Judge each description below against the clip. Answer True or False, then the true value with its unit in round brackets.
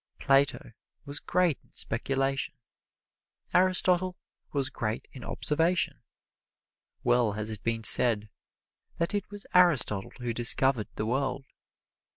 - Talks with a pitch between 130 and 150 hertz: True (135 Hz)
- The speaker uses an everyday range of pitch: False (6.5 semitones)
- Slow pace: True (115 wpm)